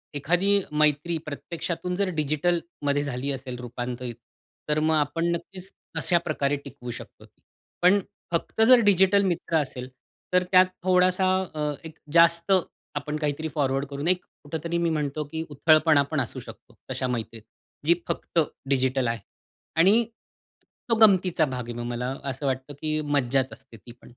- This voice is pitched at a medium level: Yes, medium, 150 Hz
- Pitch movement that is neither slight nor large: Yes, average, 4.3 semitones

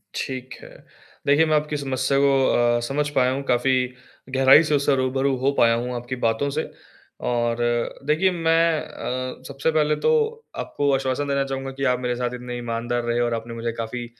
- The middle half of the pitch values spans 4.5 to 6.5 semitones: No, average, 2.8 semitones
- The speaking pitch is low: Yes, low, 130 Hz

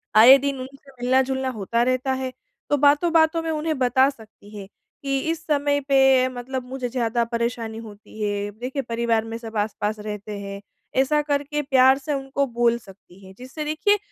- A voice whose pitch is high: Yes, very high, 255 Hz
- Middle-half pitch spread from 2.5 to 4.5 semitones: Yes, average, 3.7 semitones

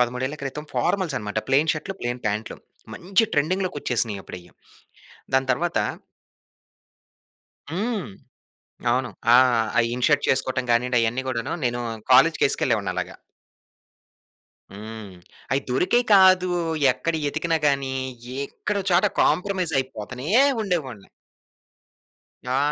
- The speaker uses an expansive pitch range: Yes, wide, 5.8 semitones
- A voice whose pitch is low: Yes, low, 130 Hz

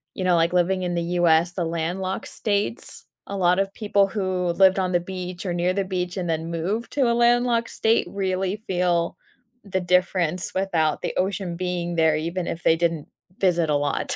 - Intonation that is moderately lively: No, narrow, 2.1 semitones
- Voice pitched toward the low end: No, medium, 180 Hz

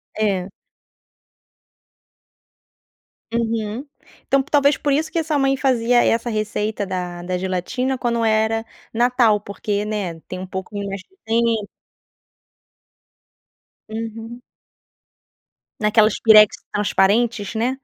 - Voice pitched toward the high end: Yes, high, 220 Hz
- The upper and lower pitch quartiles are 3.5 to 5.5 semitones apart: No, average, 2.9 semitones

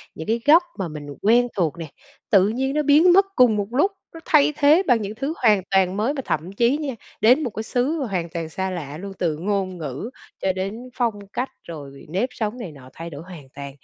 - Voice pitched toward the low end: No, high, 205 Hz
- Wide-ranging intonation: Yes, wide, 6.9 semitones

